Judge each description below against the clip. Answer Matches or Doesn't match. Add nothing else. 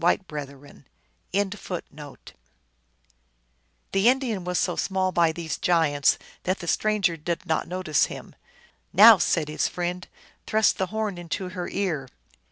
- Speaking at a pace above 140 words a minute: Doesn't match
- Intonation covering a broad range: Doesn't match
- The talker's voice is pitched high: Doesn't match